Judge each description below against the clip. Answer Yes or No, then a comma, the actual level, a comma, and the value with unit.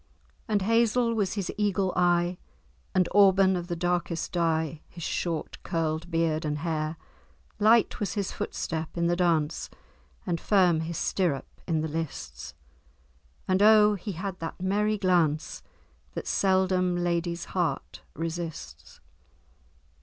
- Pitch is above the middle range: No, medium, 175 Hz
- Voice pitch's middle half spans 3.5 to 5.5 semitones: No, average, 2.8 semitones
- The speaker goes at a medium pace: No, slow, 130 wpm